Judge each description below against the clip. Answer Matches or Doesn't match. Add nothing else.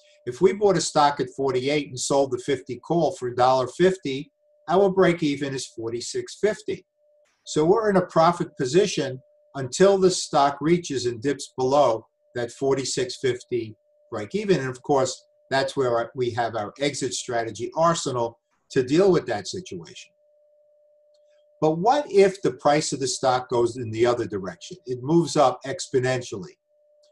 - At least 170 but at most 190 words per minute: Doesn't match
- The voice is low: Doesn't match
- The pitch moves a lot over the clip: Matches